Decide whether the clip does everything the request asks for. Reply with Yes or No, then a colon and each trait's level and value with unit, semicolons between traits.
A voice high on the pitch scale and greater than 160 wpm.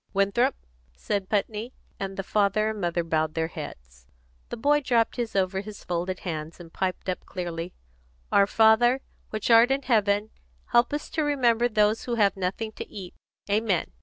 Yes: high, 205 Hz; average, 170 wpm